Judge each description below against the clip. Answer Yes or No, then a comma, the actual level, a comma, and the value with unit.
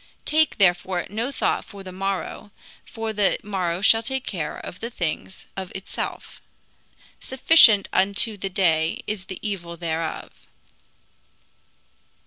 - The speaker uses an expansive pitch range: No, average, 3.7 semitones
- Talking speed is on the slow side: Yes, slow, 125 wpm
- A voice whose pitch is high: Yes, high, 195 Hz